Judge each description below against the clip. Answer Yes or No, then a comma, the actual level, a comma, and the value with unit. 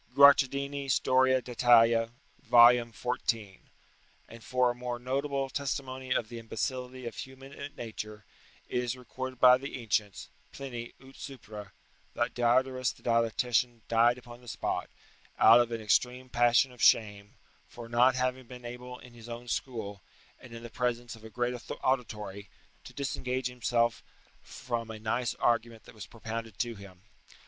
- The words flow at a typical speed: Yes, average, 155 wpm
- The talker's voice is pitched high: No, low, 120 Hz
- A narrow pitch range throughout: Yes, narrow, 1.8 semitones